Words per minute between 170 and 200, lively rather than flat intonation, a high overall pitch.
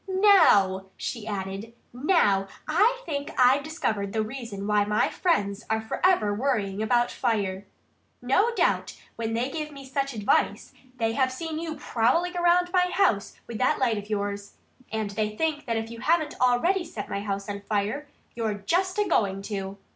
Yes: average, 175 wpm; wide, 7.3 semitones; high, 230 Hz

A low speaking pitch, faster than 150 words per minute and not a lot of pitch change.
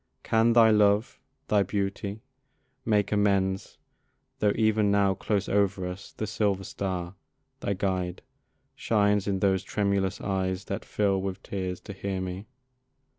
No: low, 100 Hz; slow, 135 wpm; narrow, 1.4 semitones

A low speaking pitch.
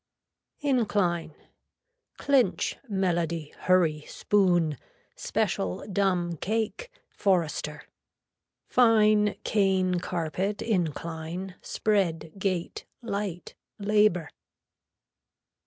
No: medium, 185 Hz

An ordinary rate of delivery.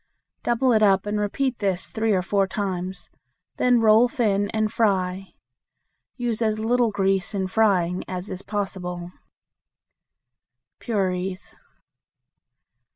No: slow, 115 wpm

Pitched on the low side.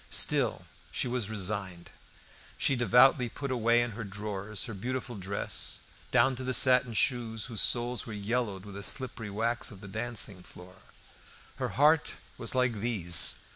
Yes: low, 115 Hz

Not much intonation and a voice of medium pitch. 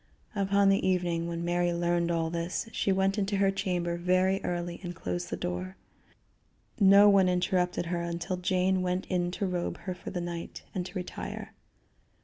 Yes: narrow, 1.7 semitones; medium, 180 Hz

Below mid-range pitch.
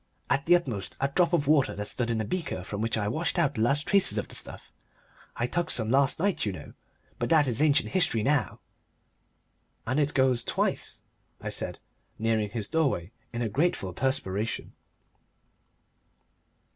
Yes: low, 130 Hz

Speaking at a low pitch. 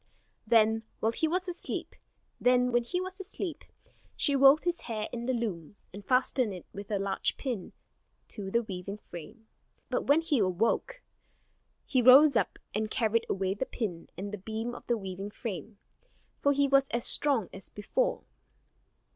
No: high, 225 Hz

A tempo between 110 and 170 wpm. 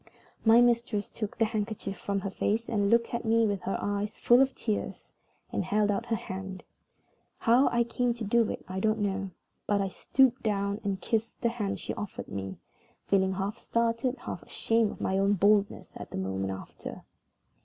No: average, 185 wpm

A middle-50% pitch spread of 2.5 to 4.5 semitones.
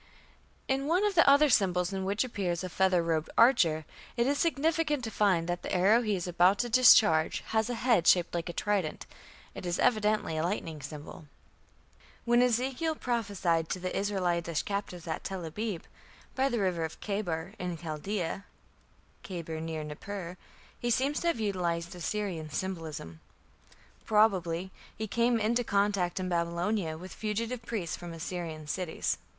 No: average, 4.9 semitones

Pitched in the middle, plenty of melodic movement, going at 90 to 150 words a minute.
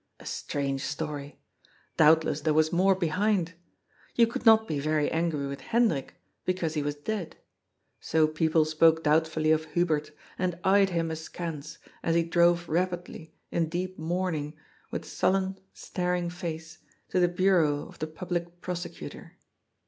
No: medium, 165 Hz; narrow, 2.4 semitones; average, 145 wpm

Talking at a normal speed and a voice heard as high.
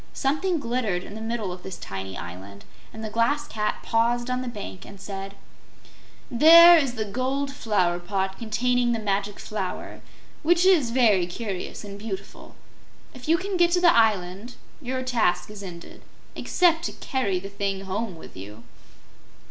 Yes: average, 165 wpm; high, 220 Hz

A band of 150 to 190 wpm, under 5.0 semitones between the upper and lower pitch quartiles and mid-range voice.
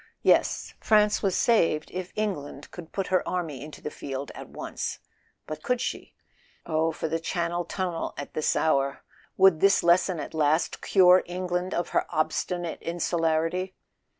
Yes: average, 155 wpm; average, 2.9 semitones; medium, 170 Hz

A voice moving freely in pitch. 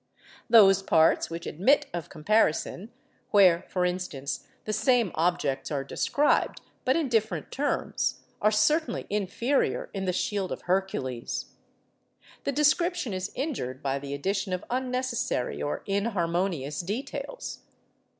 Yes: wide, 6.7 semitones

